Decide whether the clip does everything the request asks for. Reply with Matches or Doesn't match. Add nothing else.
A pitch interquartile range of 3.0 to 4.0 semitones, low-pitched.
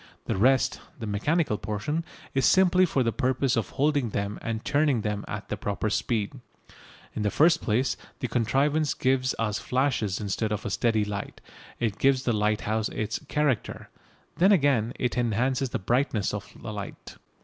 Doesn't match